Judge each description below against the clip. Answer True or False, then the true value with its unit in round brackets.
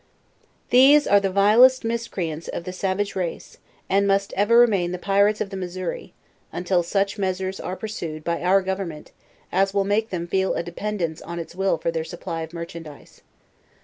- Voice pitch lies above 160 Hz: True (190 Hz)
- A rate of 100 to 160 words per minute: False (180 wpm)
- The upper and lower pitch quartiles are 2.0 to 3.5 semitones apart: True (2.8 semitones)